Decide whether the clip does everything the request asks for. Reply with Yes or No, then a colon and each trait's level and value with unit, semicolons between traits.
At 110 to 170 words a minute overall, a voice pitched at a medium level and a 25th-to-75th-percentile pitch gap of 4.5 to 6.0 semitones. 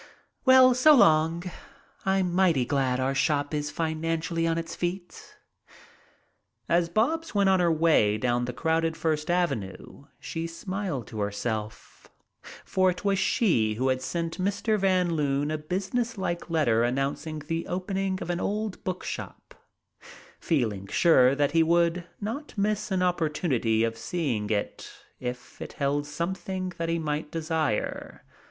Yes: average, 145 wpm; medium, 165 Hz; average, 5.1 semitones